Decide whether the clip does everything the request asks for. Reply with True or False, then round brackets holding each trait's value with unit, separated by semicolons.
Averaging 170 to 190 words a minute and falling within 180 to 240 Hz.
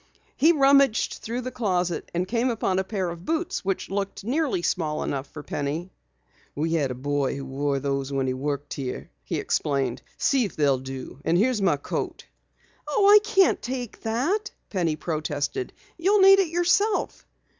True (175 wpm; 185 Hz)